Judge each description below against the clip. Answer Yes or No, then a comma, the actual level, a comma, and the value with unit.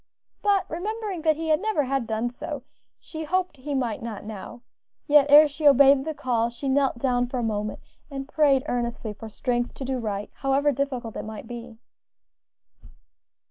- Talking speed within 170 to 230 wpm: Yes, average, 175 wpm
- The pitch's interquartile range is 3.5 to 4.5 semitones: Yes, average, 3.9 semitones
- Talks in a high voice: Yes, very high, 270 Hz